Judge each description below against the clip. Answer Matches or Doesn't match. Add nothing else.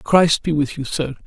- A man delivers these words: Matches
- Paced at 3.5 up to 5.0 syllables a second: Matches